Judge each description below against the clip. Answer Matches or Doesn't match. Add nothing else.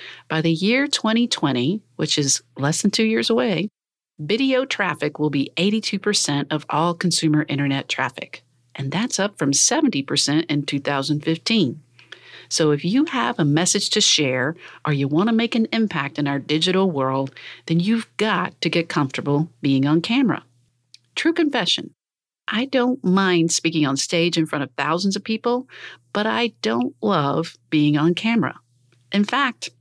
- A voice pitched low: Doesn't match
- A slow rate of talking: Doesn't match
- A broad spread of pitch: Matches